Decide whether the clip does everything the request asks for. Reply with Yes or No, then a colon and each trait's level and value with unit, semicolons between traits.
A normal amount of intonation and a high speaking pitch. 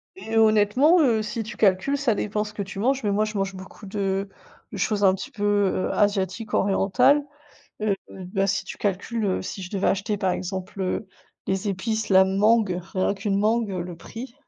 No: narrow, 2.3 semitones; high, 205 Hz